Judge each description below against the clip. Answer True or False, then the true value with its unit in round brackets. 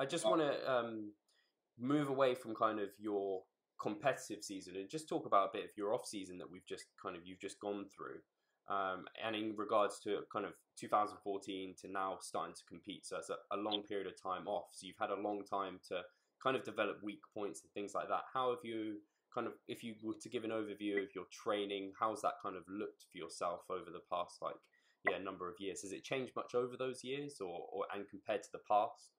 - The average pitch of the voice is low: True (105 Hz)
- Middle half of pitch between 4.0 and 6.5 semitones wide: False (3.2 semitones)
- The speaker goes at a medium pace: False (240 wpm)